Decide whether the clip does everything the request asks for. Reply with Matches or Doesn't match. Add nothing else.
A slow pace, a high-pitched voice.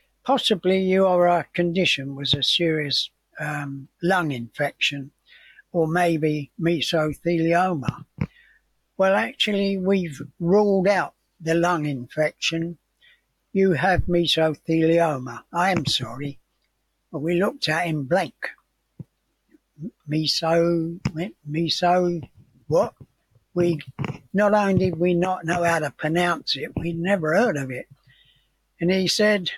Doesn't match